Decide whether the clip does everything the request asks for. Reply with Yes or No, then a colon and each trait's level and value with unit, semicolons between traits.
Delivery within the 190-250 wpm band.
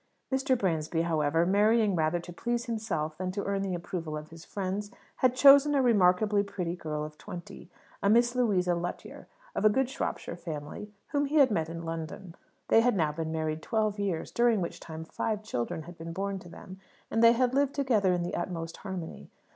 Yes: average, 200 wpm